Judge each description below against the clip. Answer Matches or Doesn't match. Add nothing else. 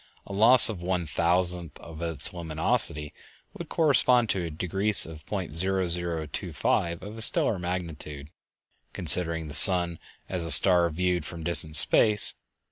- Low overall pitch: Matches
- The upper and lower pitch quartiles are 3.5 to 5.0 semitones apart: Doesn't match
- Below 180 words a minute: Matches